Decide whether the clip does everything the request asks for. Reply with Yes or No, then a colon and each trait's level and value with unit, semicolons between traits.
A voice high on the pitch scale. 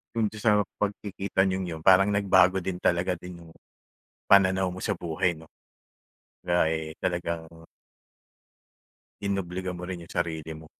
No: very low, 90 Hz